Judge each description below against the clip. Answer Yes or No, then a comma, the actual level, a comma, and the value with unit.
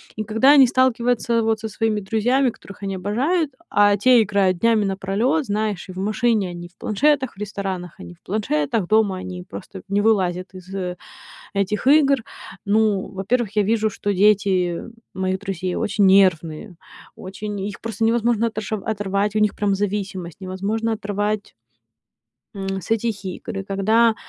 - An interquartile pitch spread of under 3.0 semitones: Yes, narrow, 2.6 semitones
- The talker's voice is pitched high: Yes, high, 205 Hz